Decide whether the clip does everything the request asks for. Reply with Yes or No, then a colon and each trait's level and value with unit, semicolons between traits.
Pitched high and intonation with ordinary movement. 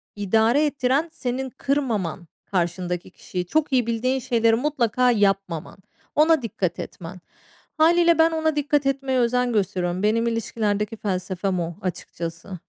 No: high, 230 Hz; wide, 6.3 semitones